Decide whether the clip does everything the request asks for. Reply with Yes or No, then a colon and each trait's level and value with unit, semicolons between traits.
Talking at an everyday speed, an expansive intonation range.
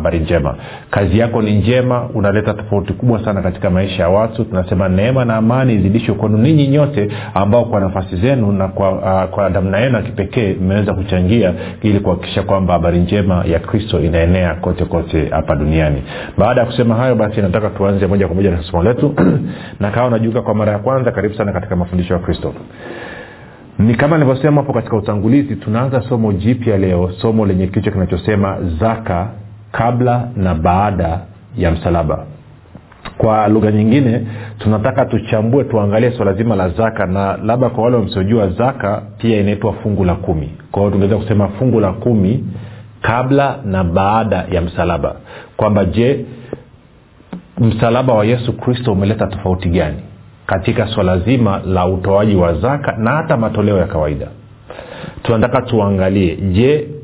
No: average, 125 wpm; average, 3.4 semitones